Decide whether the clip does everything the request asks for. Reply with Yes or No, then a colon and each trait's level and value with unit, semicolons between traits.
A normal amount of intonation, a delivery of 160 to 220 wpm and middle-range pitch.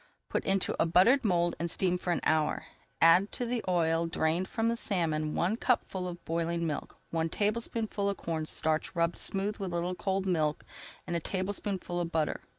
Yes: average, 3.0 semitones; average, 185 wpm; medium, 175 Hz